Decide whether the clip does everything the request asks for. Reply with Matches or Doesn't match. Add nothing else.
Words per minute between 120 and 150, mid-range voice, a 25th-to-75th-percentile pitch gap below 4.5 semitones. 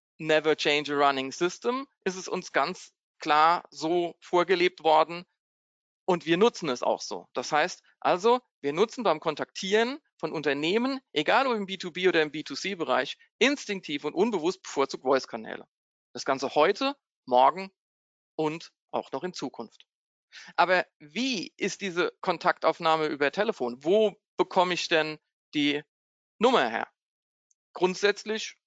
Doesn't match